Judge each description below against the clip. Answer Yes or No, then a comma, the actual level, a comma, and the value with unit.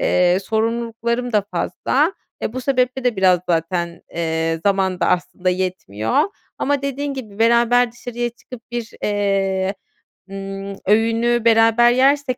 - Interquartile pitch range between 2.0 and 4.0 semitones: No, average, 4.4 semitones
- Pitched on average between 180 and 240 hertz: Yes, high, 225 Hz